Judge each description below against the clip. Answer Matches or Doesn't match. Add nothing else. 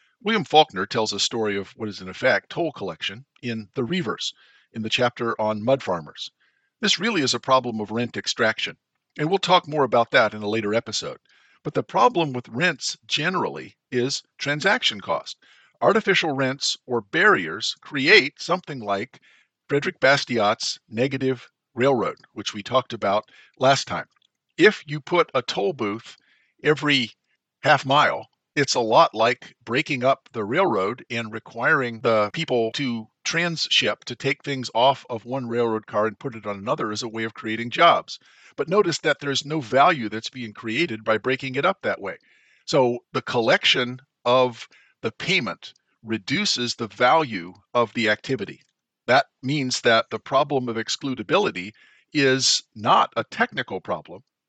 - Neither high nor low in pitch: Doesn't match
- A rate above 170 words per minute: Doesn't match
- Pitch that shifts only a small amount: Doesn't match